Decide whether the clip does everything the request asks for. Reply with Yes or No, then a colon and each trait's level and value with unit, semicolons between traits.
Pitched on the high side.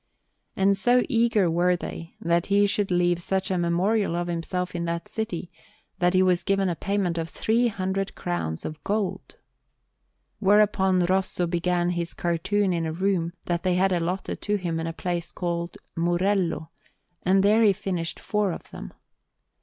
No: medium, 180 Hz